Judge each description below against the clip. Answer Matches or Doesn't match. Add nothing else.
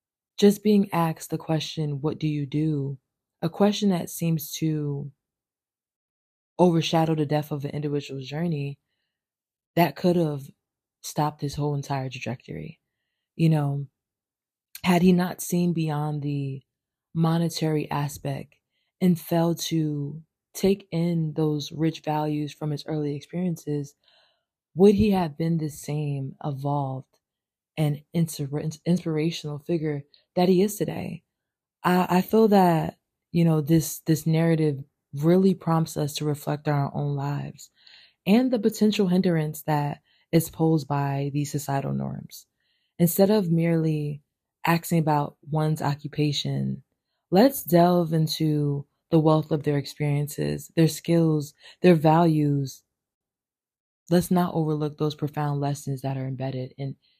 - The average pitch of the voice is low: Doesn't match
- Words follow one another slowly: Matches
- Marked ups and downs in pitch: Doesn't match